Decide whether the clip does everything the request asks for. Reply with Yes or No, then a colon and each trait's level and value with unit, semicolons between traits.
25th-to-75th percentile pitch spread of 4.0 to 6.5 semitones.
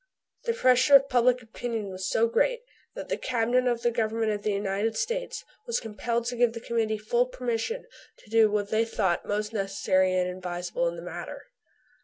No: average, 3.3 semitones